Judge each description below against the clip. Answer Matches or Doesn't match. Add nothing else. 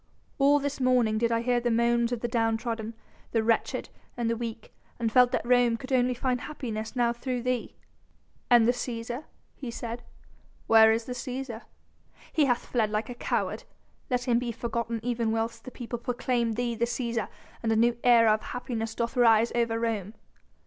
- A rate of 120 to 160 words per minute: Doesn't match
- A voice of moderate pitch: Doesn't match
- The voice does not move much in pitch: Matches